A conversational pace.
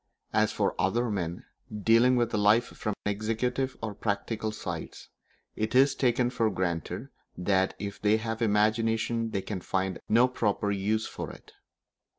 Yes: average, 155 wpm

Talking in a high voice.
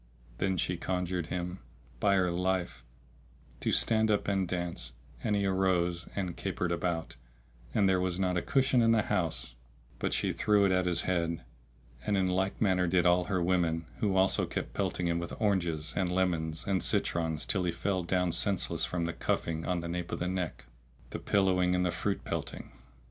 No: very low, 90 Hz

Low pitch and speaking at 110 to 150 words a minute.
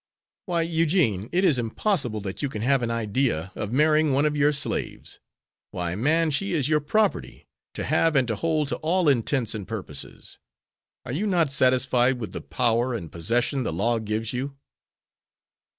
No: low, 130 Hz; average, 175 wpm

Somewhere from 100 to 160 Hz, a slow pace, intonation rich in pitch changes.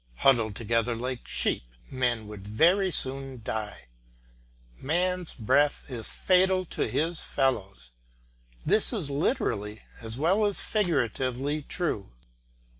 Yes: low, 135 Hz; slow, 115 wpm; wide, 7.4 semitones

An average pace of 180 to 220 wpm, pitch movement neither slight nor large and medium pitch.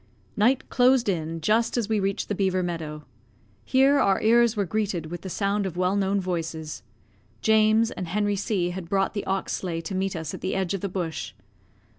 No: average, 200 wpm; average, 3.6 semitones; high, 195 Hz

